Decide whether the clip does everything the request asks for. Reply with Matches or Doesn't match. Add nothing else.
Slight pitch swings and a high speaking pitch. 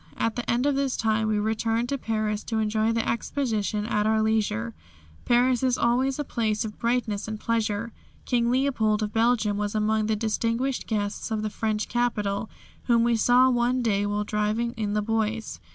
Matches